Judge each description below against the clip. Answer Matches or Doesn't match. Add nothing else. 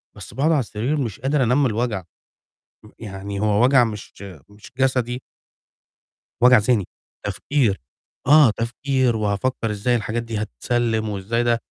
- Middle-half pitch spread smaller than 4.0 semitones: Matches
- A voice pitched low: Matches